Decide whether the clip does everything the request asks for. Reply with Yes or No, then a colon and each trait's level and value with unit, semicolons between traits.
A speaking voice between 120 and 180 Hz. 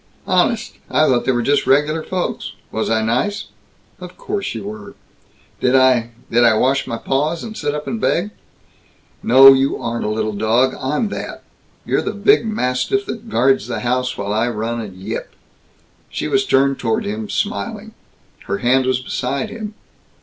Yes: low, 135 Hz